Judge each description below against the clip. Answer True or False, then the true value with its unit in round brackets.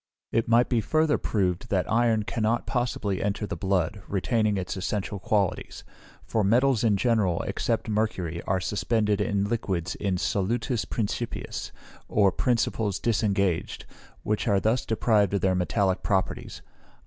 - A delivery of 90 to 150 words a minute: True (140 wpm)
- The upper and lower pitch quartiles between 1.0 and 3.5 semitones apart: True (2.9 semitones)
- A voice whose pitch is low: True (105 Hz)